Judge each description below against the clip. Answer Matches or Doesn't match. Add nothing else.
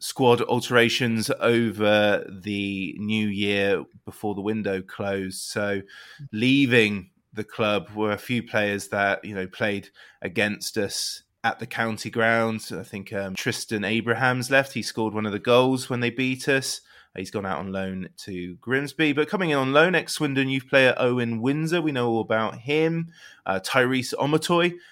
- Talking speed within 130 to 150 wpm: Doesn't match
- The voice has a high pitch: Doesn't match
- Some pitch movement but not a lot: Matches